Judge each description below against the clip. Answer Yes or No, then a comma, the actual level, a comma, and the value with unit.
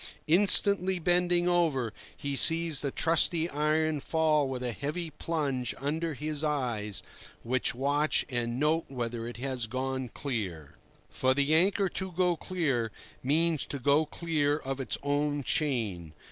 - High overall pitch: No, medium, 145 Hz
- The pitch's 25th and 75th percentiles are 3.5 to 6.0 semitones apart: Yes, average, 4.1 semitones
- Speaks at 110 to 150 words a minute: Yes, average, 145 wpm